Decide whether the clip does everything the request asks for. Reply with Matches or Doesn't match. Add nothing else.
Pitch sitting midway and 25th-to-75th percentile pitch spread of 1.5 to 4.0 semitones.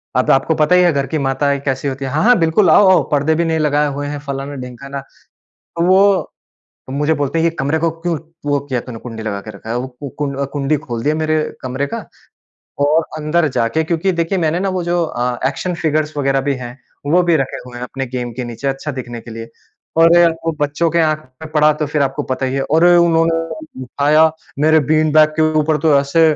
Matches